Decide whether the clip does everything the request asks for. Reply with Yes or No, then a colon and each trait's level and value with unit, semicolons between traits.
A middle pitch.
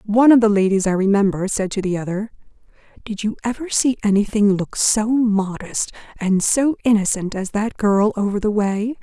No: high, 210 Hz